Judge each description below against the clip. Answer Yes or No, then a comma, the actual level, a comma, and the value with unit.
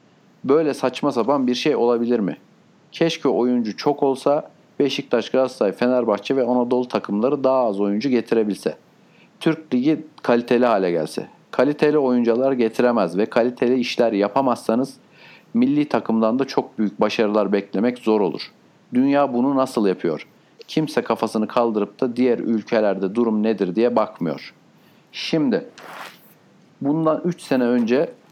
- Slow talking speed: No, average, 130 wpm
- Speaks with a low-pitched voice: Yes, low, 125 Hz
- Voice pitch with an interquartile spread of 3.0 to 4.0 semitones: Yes, average, 3.3 semitones